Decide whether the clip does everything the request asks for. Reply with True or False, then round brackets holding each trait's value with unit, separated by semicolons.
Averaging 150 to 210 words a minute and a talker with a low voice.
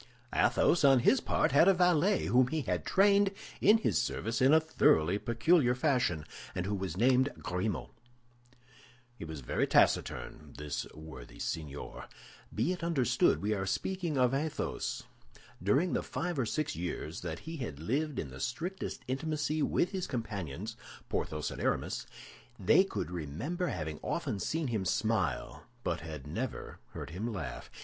True (155 wpm; 120 Hz)